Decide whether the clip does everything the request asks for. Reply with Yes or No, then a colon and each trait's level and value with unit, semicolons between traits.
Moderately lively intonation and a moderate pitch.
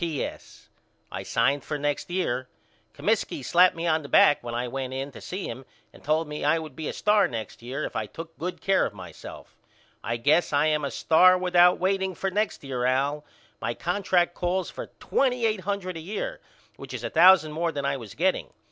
Yes: average, 4.9 semitones; medium, 160 Hz